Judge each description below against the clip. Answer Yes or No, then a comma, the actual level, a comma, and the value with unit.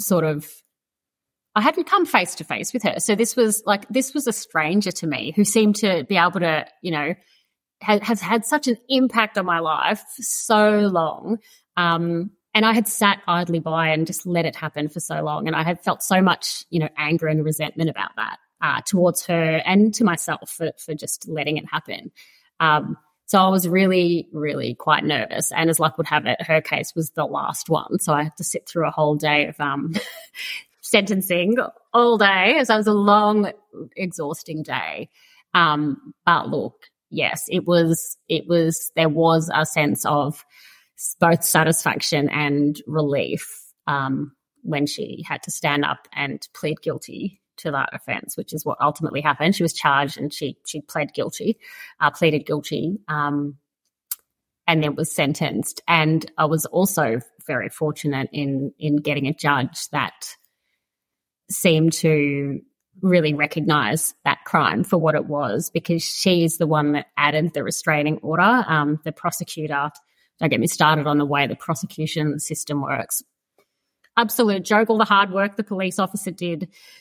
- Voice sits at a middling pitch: Yes, medium, 165 Hz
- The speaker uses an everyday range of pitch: Yes, average, 4.7 semitones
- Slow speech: No, average, 175 wpm